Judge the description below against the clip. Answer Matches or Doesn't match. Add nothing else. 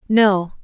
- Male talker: Doesn't match